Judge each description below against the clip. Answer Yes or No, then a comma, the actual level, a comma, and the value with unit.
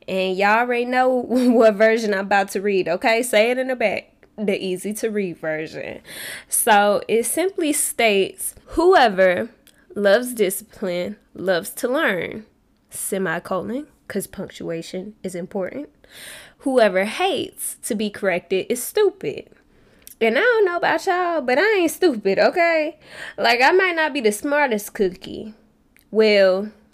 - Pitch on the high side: Yes, high, 220 Hz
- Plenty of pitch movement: Yes, wide, 6.5 semitones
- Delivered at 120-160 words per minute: Yes, average, 140 wpm